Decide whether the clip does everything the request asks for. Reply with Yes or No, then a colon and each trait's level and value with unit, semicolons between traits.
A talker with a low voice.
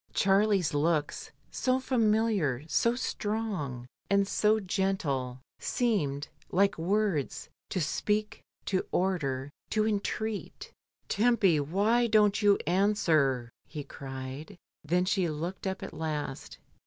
No: high, 190 Hz